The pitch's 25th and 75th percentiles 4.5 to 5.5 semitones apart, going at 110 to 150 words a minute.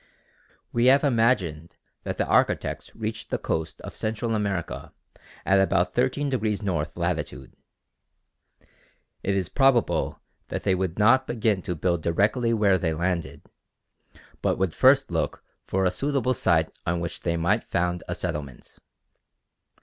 Yes: average, 5.1 semitones; slow, 135 wpm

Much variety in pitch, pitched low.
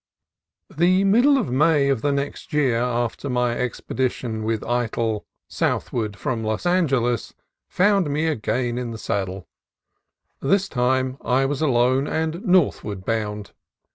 No: average, 4.9 semitones; low, 130 Hz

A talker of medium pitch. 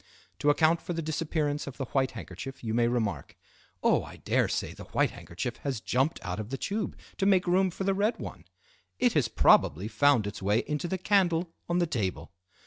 Yes: medium, 145 Hz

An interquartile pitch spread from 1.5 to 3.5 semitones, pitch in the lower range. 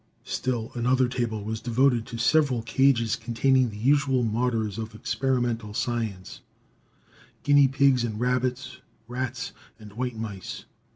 Yes: narrow, 2.5 semitones; low, 120 Hz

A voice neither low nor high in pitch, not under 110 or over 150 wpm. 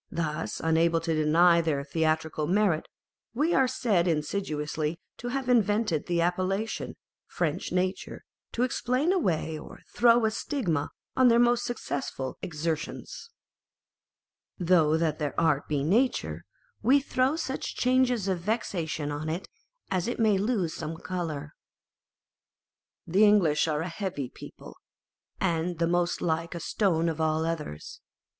Yes: medium, 170 Hz; average, 140 wpm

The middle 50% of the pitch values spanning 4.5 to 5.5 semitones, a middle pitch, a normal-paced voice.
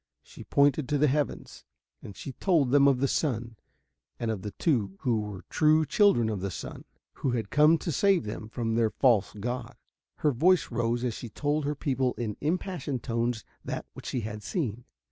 No: average, 4.8 semitones; low, 125 Hz; average, 195 wpm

